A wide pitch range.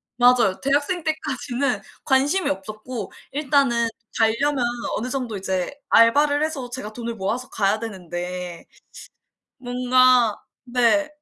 No: average, 4.3 semitones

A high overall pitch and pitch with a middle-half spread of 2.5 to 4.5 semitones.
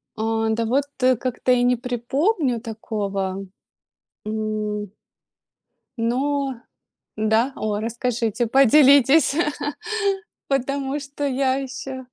Yes: high, 245 Hz; average, 3.6 semitones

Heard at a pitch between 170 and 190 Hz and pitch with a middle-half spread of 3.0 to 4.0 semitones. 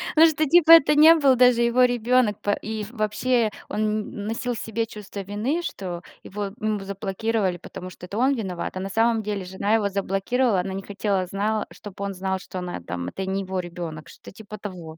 No: high, 210 Hz; average, 3.6 semitones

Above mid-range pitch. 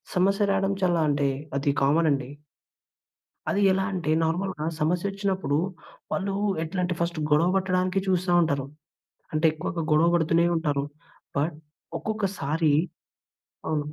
No: medium, 170 Hz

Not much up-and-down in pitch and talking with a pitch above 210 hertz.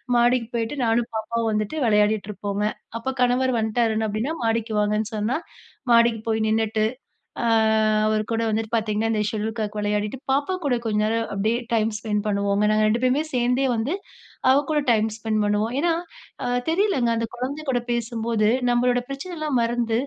Yes: narrow, 2.3 semitones; high, 225 Hz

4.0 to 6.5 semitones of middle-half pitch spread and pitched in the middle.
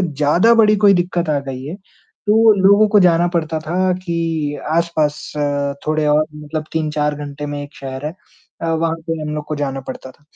No: average, 3.0 semitones; medium, 155 Hz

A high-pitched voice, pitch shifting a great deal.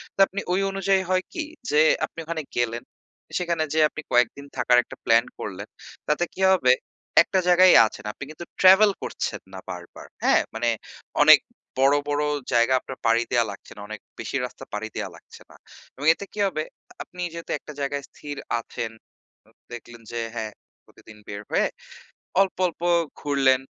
No: medium, 140 Hz; wide, 6.8 semitones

